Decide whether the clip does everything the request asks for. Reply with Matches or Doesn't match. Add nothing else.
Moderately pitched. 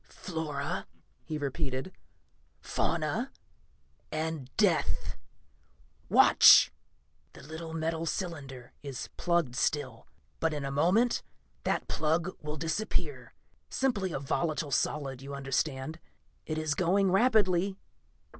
Matches